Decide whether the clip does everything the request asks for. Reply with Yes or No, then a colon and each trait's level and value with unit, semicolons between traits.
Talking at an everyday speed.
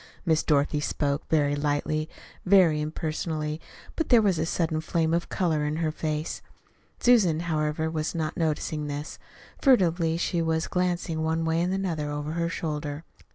Yes: average, 155 wpm